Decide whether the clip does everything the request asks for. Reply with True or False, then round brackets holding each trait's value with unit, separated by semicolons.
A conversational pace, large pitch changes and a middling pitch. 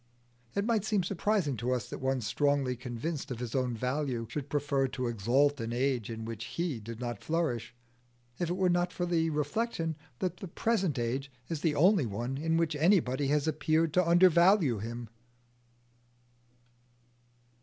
True (165 wpm; 5.7 semitones; 145 Hz)